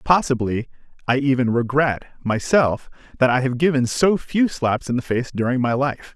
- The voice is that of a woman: No, male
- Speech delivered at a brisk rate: No, average, 175 wpm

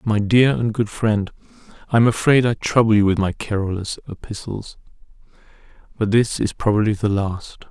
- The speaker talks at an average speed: Yes, average, 165 wpm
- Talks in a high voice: No, low, 110 Hz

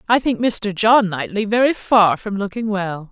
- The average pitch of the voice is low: No, high, 210 Hz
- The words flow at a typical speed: Yes, average, 195 wpm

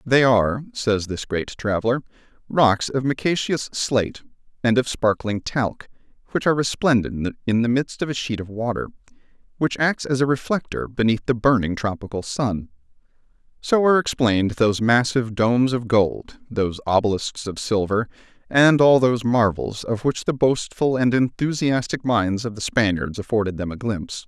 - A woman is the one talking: No, male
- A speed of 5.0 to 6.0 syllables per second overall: Yes, 5.1 syllables/s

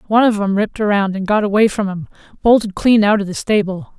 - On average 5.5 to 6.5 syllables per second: Yes, 6.4 syllables/s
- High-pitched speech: Yes, high, 205 Hz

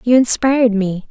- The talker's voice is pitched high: Yes, high, 230 Hz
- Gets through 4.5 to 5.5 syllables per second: Yes, 5.0 syllables/s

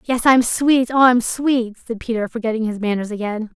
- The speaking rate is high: Yes, fast, 220 wpm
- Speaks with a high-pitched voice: Yes, high, 230 Hz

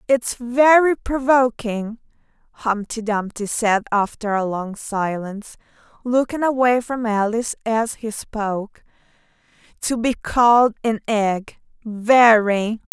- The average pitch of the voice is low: No, high, 225 Hz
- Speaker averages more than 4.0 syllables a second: No, 3.8 syllables/s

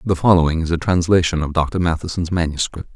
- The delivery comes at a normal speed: Yes, average, 185 wpm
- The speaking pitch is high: No, very low, 85 Hz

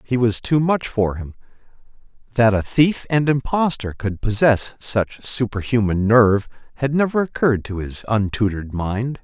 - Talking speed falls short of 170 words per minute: Yes, average, 150 wpm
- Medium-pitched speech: No, low, 115 Hz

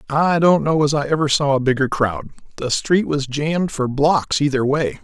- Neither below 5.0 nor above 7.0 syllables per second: No, 4.8 syllables/s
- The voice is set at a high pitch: No, medium, 145 Hz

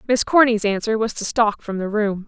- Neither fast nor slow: No, fast, 240 wpm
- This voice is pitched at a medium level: No, high, 215 Hz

